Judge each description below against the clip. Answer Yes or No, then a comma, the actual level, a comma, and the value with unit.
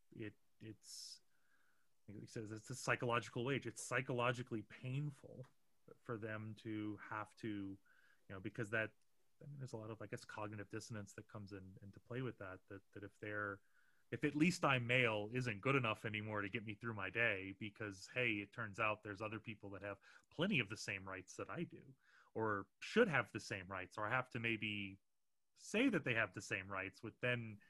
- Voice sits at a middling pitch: No, low, 110 Hz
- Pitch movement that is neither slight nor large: Yes, average, 3.0 semitones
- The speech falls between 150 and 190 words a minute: No, fast, 205 wpm